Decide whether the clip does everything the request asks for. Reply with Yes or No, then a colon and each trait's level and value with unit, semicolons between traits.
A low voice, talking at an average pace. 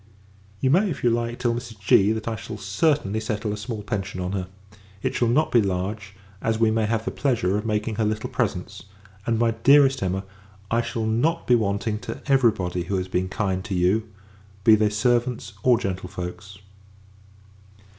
Yes: low, 110 Hz; average, 190 wpm